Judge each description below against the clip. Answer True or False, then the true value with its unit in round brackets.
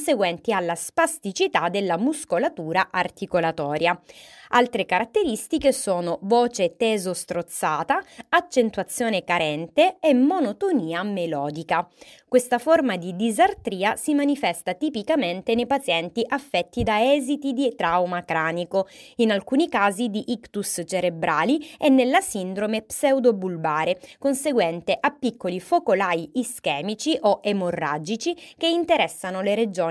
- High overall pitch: True (215 Hz)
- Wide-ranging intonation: True (7.6 semitones)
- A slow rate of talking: True (100 wpm)